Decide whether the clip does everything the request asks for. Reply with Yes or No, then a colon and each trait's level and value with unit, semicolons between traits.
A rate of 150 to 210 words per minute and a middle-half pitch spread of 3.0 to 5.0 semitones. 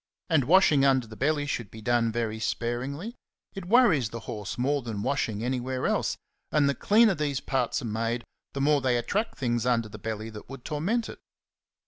Yes: average, 190 wpm; average, 4.2 semitones